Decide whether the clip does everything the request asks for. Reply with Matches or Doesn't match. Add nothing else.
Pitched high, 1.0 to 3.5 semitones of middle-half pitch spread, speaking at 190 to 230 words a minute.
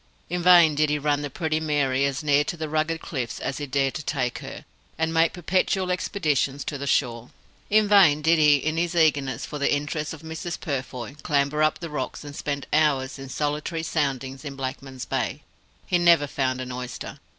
Doesn't match